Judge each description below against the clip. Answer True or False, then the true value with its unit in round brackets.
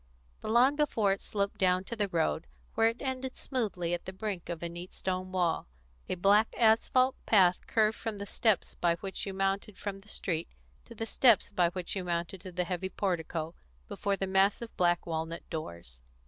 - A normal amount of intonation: True (3.6 semitones)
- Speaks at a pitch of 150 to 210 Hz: True (190 Hz)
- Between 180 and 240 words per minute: True (195 wpm)